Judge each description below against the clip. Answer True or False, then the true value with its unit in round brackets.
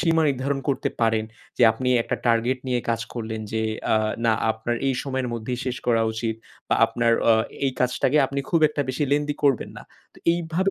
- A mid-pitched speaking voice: False (125 Hz)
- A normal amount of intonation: True (3.4 semitones)